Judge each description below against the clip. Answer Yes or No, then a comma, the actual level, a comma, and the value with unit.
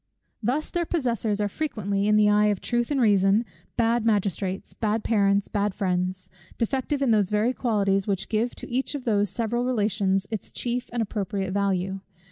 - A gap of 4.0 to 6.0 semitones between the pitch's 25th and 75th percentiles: No, average, 3.3 semitones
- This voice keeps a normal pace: Yes, average, 175 wpm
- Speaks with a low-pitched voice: No, high, 210 Hz